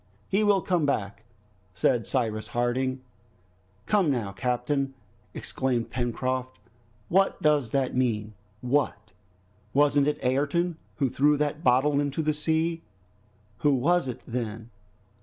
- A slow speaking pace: Yes, slow, 120 wpm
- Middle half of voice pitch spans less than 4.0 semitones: Yes, average, 3.6 semitones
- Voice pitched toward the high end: No, low, 135 Hz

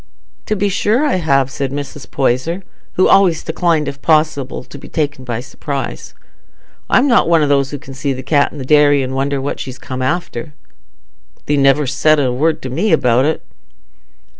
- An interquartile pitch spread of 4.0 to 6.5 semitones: No, average, 3.3 semitones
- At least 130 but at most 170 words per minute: No, average, 190 wpm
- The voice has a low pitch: No, medium, 145 Hz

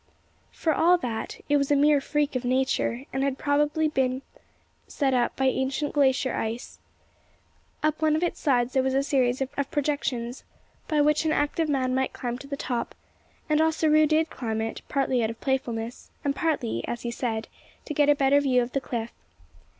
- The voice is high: Yes, very high, 275 Hz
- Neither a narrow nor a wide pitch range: Yes, average, 3.0 semitones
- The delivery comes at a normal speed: Yes, average, 190 wpm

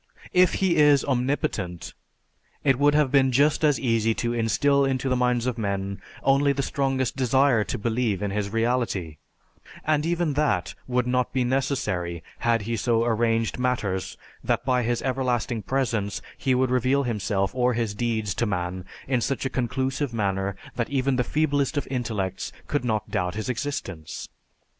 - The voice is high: No, low, 125 Hz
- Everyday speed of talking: Yes, average, 165 wpm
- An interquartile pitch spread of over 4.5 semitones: No, average, 3.8 semitones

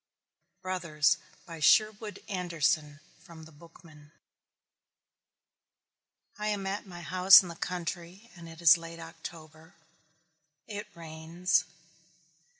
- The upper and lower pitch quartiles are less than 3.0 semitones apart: Yes, narrow, 2.6 semitones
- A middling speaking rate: No, slow, 105 wpm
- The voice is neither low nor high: Yes, medium, 170 Hz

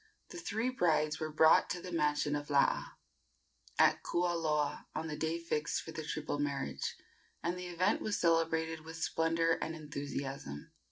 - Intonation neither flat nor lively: No, narrow, 2.1 semitones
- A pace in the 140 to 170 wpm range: Yes, average, 160 wpm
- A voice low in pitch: No, medium, 160 Hz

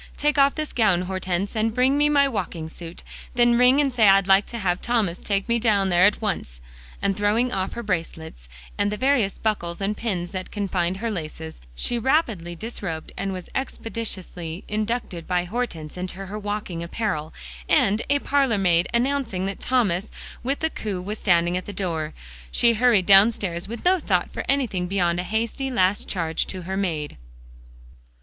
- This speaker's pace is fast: No, average, 175 wpm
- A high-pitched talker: Yes, high, 200 Hz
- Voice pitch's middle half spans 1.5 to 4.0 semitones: No, average, 4.8 semitones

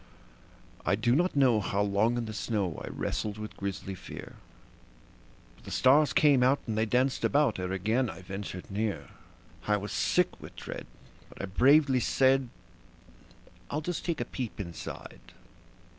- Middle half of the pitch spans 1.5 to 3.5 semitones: No, average, 4.9 semitones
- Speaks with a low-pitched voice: Yes, low, 110 Hz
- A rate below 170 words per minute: Yes, average, 160 wpm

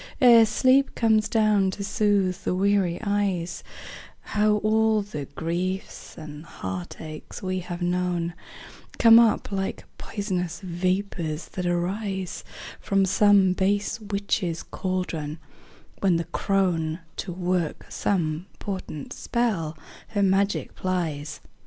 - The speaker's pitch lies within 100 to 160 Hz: No, medium, 185 Hz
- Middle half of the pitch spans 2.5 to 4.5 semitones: Yes, average, 2.9 semitones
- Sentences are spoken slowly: Yes, slow, 115 wpm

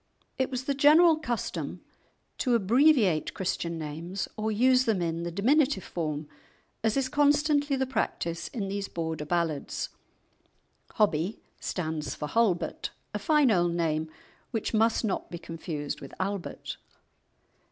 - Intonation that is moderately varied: No, wide, 7.6 semitones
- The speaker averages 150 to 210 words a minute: No, slow, 135 wpm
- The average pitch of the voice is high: Yes, high, 200 Hz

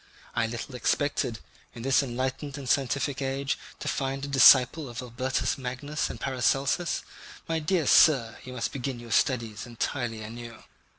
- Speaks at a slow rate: No, average, 155 wpm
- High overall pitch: No, low, 130 Hz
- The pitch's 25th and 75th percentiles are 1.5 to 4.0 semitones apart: Yes, average, 2.7 semitones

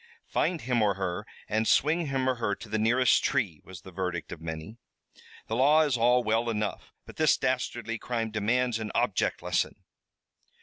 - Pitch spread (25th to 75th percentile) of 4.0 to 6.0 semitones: No, average, 3.6 semitones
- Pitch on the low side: Yes, low, 115 Hz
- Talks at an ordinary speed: Yes, average, 180 wpm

